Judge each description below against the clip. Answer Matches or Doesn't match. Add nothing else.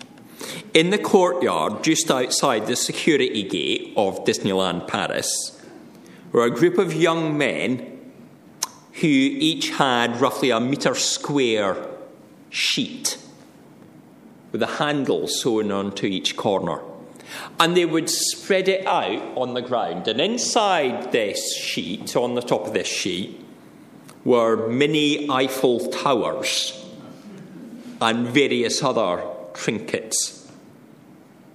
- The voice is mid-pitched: Matches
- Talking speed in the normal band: Doesn't match